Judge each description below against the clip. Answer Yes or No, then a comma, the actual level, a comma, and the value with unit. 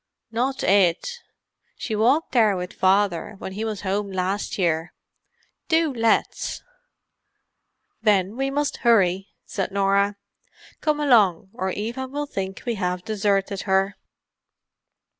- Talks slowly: Yes, slow, 120 wpm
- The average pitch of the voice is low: No, high, 205 Hz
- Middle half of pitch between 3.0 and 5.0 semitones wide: Yes, average, 3.8 semitones